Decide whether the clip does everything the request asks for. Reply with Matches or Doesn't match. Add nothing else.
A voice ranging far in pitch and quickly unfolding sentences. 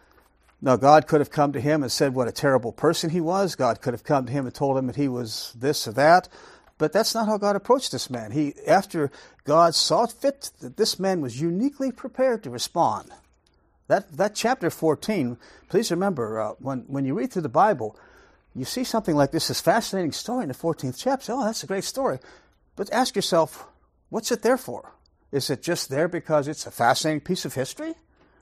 Matches